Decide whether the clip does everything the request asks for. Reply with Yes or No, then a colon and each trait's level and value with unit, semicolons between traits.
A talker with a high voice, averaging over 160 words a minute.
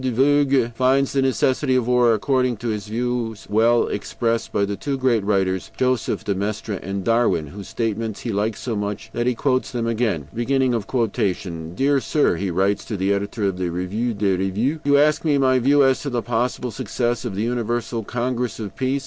No: low, 115 Hz; average, 195 wpm